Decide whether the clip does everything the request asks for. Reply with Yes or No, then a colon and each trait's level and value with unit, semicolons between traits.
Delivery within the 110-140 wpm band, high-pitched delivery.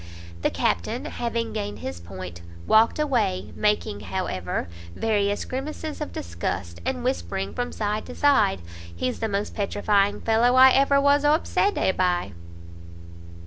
Yes: slow, 135 wpm; high, 205 Hz